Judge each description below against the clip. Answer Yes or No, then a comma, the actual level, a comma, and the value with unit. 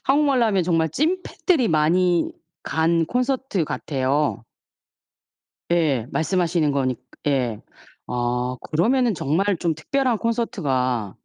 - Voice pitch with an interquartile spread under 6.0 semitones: No, wide, 8.8 semitones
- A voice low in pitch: No, medium, 165 Hz